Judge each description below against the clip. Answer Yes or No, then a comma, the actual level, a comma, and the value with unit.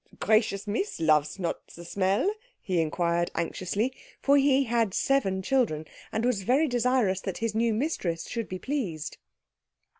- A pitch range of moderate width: No, wide, 6.4 semitones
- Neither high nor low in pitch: No, high, 210 Hz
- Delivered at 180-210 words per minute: No, average, 155 wpm